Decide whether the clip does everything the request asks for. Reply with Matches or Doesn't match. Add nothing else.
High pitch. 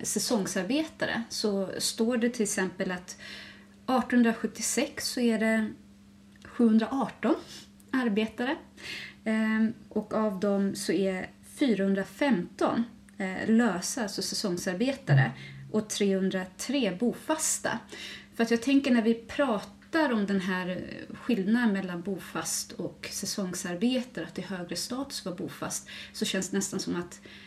Matches